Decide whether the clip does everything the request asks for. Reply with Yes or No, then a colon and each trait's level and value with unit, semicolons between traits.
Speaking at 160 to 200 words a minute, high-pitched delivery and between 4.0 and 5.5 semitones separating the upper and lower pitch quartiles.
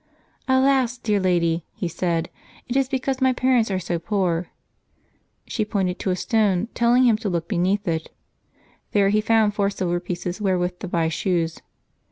Yes: average, 170 wpm; high, 195 Hz; average, 4.4 semitones